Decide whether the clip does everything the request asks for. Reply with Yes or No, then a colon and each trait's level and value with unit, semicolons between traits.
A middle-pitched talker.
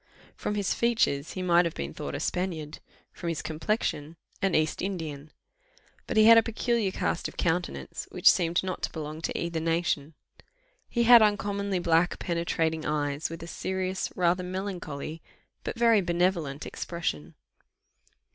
Yes: medium, 170 Hz